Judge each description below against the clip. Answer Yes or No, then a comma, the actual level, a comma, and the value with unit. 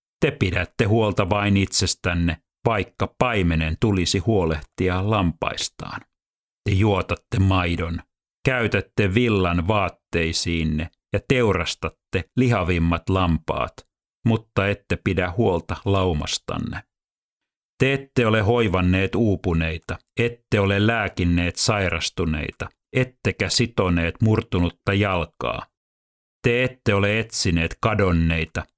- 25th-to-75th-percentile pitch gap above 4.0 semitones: Yes, average, 4.6 semitones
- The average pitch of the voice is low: Yes, very low, 95 Hz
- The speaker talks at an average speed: No, slow, 90 wpm